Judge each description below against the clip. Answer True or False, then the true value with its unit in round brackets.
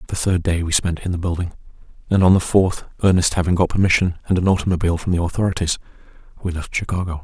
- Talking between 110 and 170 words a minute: False (205 wpm)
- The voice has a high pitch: False (90 Hz)